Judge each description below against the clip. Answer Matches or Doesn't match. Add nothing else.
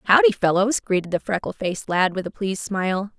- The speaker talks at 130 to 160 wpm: Doesn't match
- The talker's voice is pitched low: Doesn't match